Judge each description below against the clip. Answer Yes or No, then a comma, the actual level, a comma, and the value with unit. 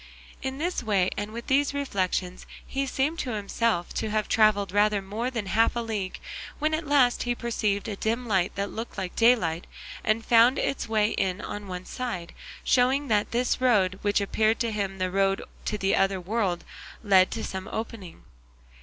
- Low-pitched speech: No, high, 215 Hz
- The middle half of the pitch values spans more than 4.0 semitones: No, average, 3.7 semitones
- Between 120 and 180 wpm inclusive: No, average, 190 wpm